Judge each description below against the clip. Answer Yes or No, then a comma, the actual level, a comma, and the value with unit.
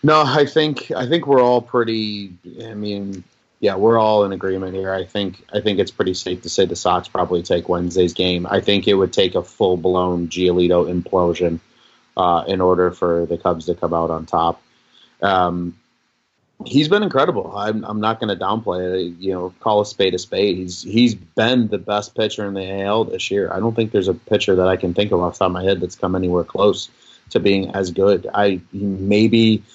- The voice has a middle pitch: No, very low, 95 Hz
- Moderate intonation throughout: Yes, average, 3.2 semitones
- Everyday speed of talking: No, fast, 215 wpm